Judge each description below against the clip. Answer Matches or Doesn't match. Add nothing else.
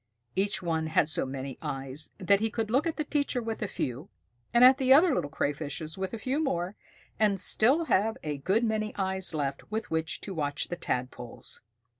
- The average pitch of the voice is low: Doesn't match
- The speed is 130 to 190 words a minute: Doesn't match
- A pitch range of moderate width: Doesn't match